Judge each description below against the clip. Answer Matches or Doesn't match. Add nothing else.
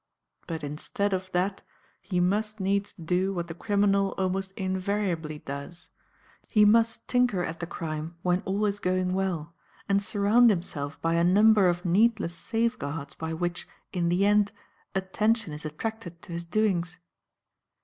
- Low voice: Doesn't match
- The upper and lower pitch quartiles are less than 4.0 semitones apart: Matches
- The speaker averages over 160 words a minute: Doesn't match